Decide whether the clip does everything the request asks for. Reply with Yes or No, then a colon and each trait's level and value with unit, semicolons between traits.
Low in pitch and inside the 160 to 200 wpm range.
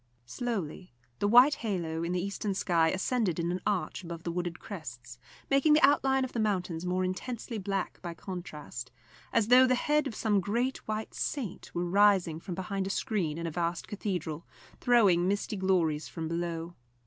No: medium, 185 Hz; average, 180 wpm